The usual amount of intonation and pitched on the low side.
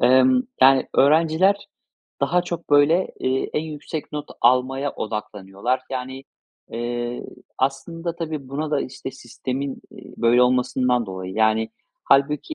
Yes: average, 3.5 semitones; low, 130 Hz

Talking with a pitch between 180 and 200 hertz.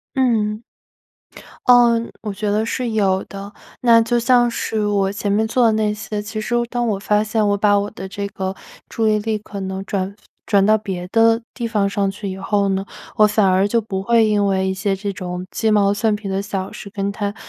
No: high, 210 Hz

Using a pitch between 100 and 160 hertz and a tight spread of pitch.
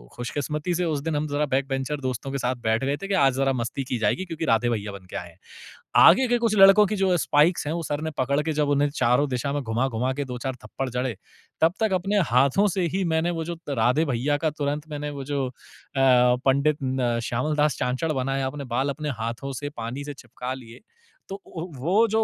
No: medium, 140 Hz; average, 4.0 semitones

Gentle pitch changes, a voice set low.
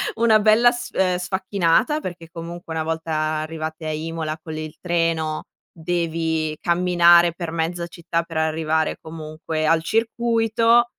No: narrow, 2.3 semitones; medium, 165 Hz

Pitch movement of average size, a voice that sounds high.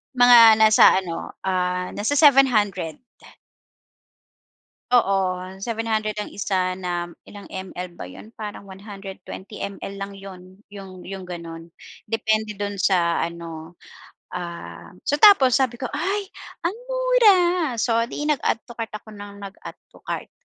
Yes: average, 3.8 semitones; high, 200 Hz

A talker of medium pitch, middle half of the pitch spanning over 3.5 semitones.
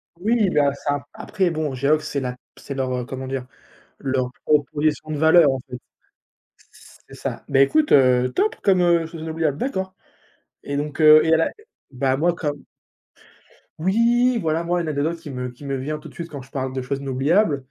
Yes: medium, 150 Hz; average, 3.9 semitones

